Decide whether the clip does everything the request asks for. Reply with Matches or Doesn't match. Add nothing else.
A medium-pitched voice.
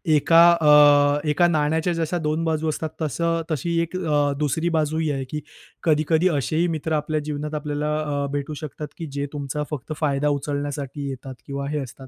Matches